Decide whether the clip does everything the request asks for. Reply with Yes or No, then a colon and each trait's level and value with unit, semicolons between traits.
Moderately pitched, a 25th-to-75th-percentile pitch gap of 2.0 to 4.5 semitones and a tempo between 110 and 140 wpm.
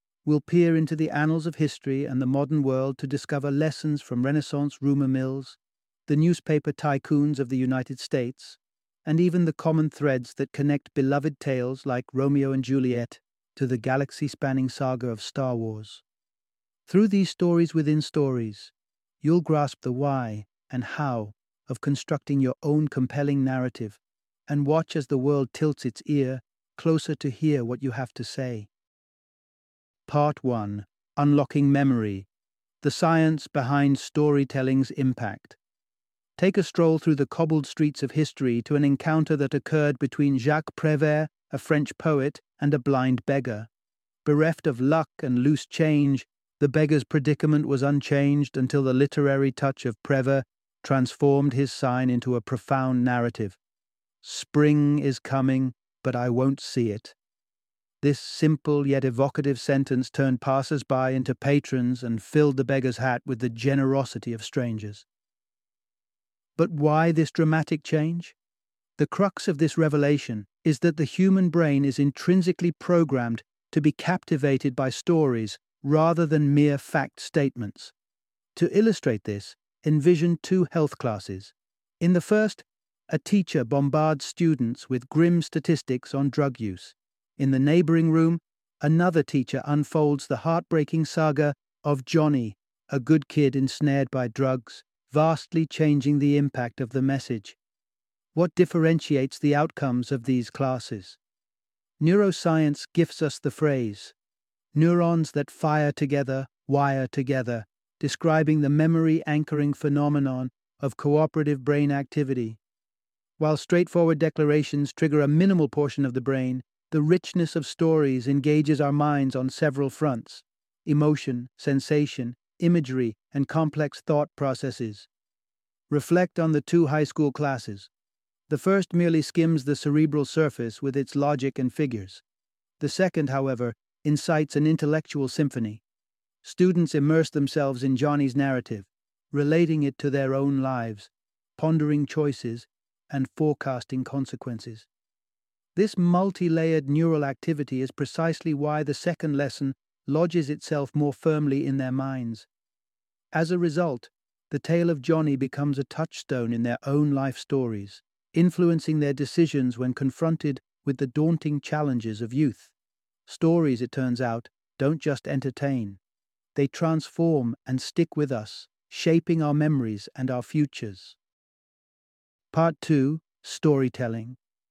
Yes: medium, 145 Hz; average, 3.0 semitones; slow, 135 wpm